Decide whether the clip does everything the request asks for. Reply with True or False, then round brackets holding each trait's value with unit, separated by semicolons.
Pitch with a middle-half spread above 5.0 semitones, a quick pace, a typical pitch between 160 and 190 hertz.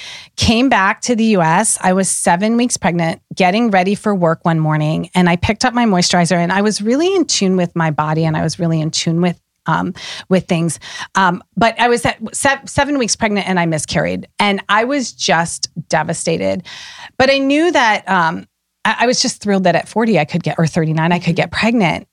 True (5.4 semitones; 220 wpm; 185 Hz)